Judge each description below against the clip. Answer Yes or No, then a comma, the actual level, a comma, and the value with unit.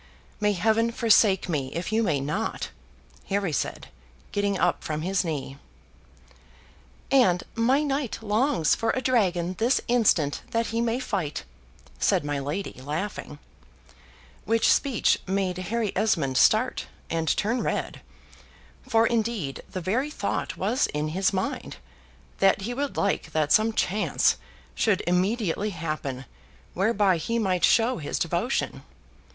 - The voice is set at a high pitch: Yes, high, 200 Hz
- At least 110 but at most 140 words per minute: Yes, slow, 135 wpm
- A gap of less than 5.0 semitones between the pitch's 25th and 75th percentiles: No, wide, 5.6 semitones